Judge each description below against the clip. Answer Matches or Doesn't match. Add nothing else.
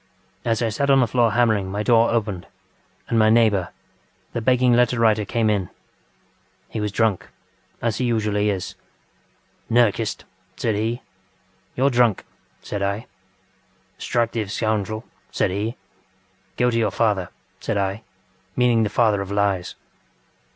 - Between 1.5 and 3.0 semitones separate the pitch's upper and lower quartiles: Matches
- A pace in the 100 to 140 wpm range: Matches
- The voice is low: Matches